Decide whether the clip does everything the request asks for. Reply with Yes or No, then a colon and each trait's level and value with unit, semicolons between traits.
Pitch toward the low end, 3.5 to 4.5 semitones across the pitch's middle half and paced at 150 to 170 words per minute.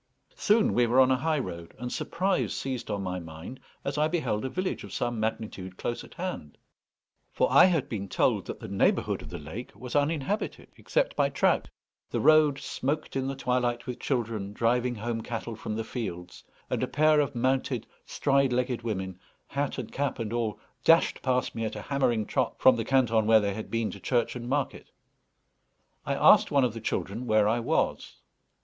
No: low, 120 Hz; average, 4.0 semitones; average, 195 wpm